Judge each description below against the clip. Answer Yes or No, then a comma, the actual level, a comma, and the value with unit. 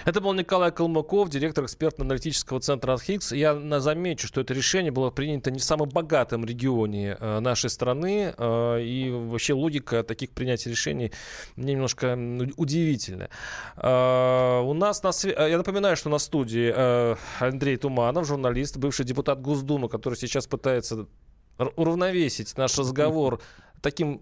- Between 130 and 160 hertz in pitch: Yes, low, 135 Hz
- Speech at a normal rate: Yes, average, 130 wpm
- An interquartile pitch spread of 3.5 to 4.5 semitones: Yes, average, 3.8 semitones